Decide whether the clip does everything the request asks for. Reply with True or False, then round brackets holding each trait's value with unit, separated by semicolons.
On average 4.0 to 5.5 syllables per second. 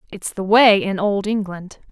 True (4.3 syllables/s)